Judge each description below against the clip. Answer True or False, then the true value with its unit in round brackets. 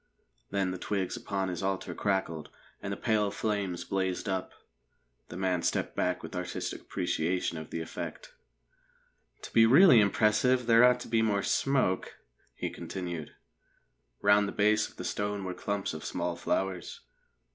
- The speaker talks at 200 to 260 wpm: False (155 wpm)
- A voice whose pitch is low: True (95 Hz)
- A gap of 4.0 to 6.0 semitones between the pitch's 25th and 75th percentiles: False (2.8 semitones)